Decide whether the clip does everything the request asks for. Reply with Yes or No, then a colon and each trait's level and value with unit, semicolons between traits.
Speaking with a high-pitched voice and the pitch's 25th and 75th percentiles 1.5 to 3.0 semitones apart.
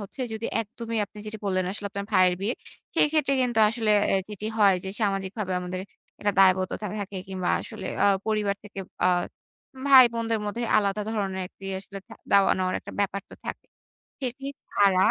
Yes: high, 205 Hz; average, 2.7 semitones